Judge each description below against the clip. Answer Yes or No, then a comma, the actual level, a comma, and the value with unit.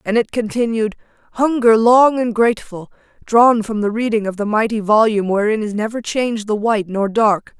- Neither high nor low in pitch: No, high, 220 Hz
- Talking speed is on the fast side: No, average, 180 wpm